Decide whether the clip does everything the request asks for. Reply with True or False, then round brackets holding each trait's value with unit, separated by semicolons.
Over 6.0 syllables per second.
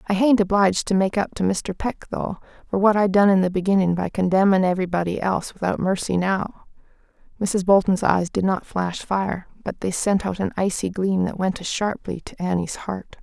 False (5.3 syllables/s)